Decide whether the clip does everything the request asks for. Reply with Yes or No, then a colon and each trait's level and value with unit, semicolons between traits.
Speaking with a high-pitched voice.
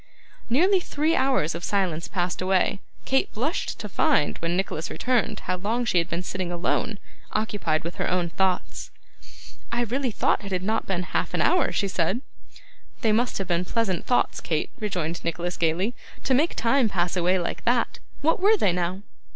Yes: high, 195 Hz